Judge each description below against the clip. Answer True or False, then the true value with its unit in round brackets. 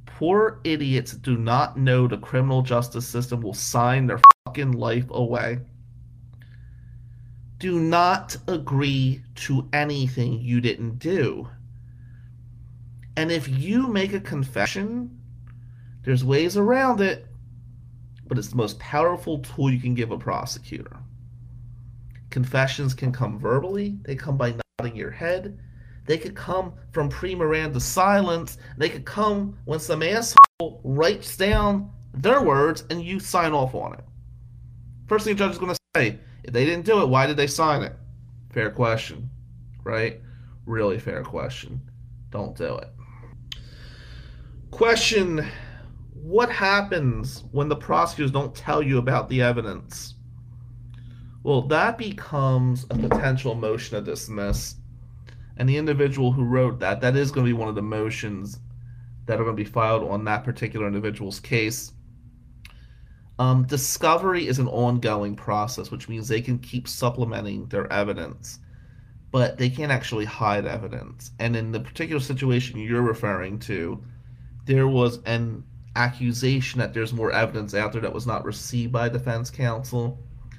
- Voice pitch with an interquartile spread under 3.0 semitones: True (2.6 semitones)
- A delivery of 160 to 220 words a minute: False (145 wpm)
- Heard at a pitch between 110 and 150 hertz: True (120 Hz)